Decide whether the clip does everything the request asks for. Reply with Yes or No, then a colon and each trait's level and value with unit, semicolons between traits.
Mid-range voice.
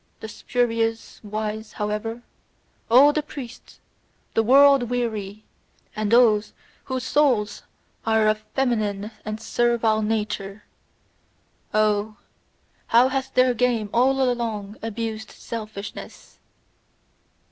No: high, 225 Hz